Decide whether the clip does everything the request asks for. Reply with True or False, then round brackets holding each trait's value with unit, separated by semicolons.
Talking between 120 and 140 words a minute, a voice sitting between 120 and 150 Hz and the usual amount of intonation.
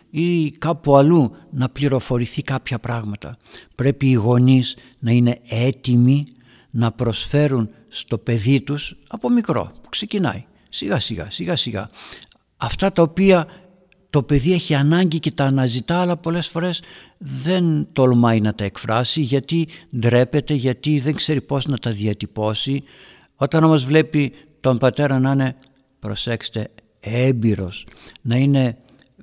True (130 wpm; 135 Hz; 4.2 semitones)